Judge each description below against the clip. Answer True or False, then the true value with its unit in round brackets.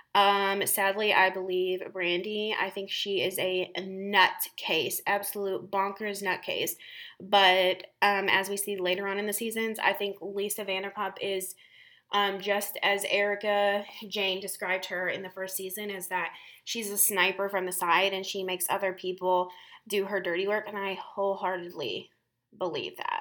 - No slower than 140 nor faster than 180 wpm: True (160 wpm)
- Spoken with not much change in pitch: True (1.5 semitones)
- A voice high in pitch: True (195 Hz)